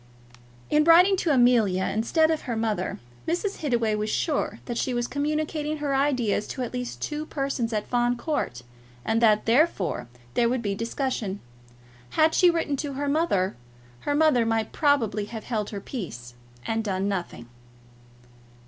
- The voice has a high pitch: Yes, high, 245 Hz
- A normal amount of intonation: No, wide, 5.7 semitones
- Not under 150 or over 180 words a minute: Yes, average, 165 wpm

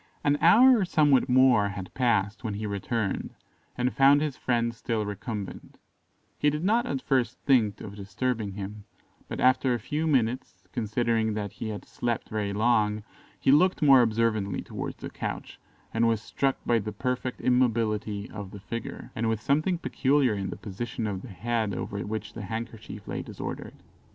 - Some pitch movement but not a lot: Yes, average, 3.7 semitones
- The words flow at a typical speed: Yes, average, 175 wpm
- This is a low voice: Yes, low, 115 Hz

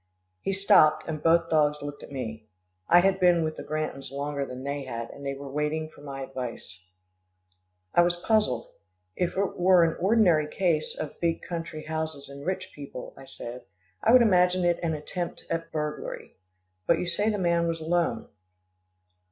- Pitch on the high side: No, medium, 160 Hz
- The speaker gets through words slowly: No, average, 180 wpm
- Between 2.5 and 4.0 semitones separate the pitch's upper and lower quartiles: Yes, average, 3.6 semitones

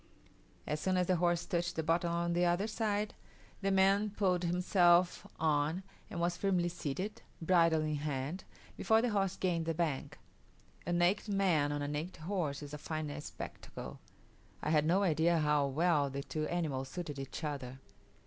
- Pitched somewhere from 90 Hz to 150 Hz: No, medium, 170 Hz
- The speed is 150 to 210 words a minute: Yes, average, 175 wpm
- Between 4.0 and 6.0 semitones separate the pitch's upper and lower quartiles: No, average, 3.4 semitones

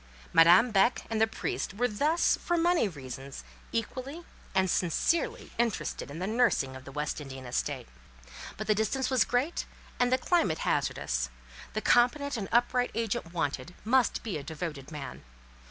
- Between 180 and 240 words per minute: No, average, 160 wpm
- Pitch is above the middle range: Yes, high, 215 Hz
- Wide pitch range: Yes, wide, 8.5 semitones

